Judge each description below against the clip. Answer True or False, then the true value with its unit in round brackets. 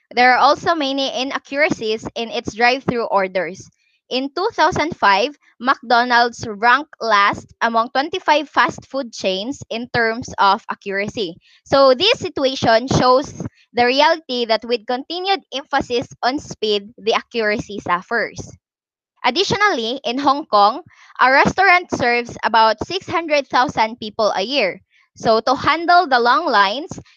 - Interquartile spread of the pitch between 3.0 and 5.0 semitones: True (4.5 semitones)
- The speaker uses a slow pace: True (125 wpm)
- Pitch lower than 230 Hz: False (250 Hz)